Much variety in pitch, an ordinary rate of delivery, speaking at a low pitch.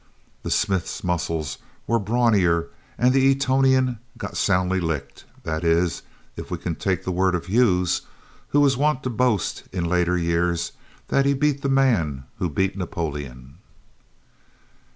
Yes: wide, 7.0 semitones; average, 150 wpm; very low, 95 Hz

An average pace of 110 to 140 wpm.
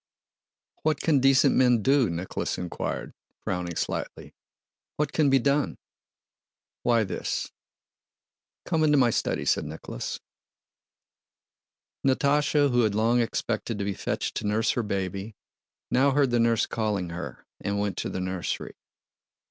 Yes: slow, 135 wpm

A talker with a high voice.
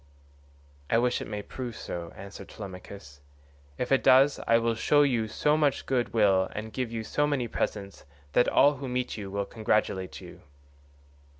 No: low, 115 Hz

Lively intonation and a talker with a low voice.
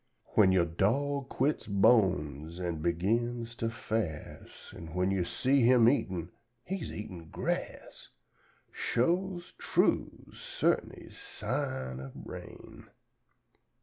Yes: wide, 6.1 semitones; low, 100 Hz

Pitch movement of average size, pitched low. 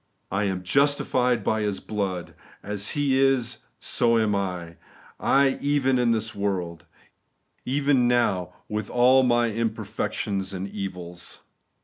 Yes: average, 4.5 semitones; low, 110 Hz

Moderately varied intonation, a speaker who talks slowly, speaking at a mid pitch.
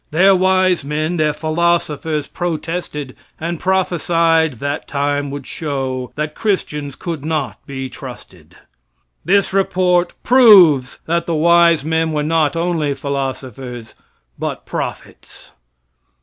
Yes: average, 3.4 semitones; slow, 115 wpm; medium, 155 Hz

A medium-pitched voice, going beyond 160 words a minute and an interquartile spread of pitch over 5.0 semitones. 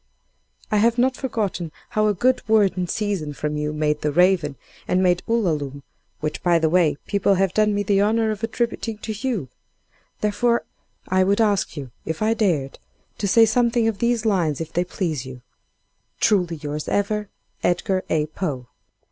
No: high, 195 Hz; average, 175 wpm; wide, 5.6 semitones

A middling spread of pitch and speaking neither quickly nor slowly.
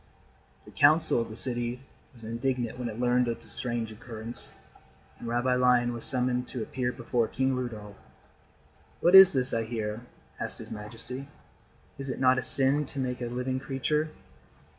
No: narrow, 2.0 semitones; average, 170 wpm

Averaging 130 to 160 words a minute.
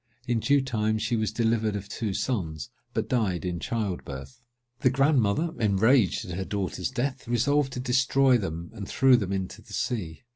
No: average, 180 wpm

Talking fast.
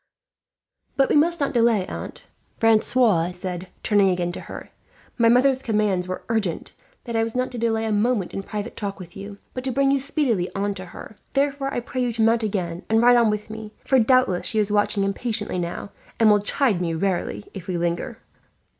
Yes: fast, 210 wpm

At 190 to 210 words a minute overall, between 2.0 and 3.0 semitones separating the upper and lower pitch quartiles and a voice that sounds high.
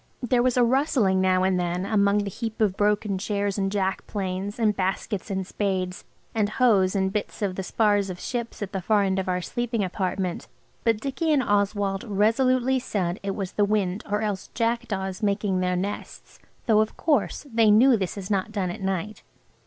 Yes: average, 195 wpm; average, 2.7 semitones; high, 205 Hz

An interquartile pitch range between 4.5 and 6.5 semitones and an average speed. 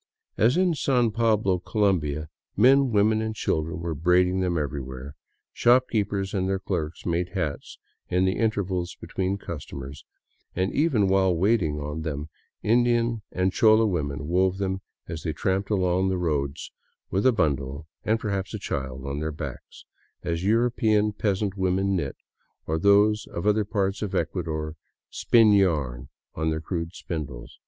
Yes: average, 5.0 semitones; average, 155 wpm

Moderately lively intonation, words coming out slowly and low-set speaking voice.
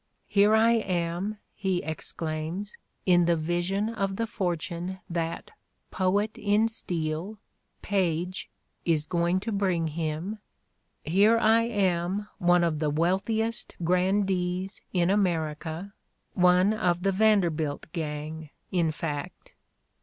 No: average, 3.5 semitones; slow, 115 wpm; medium, 180 Hz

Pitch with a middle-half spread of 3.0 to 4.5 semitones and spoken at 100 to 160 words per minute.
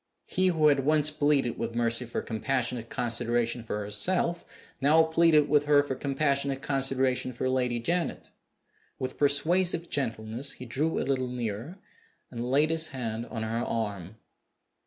Yes: average, 4.1 semitones; average, 150 wpm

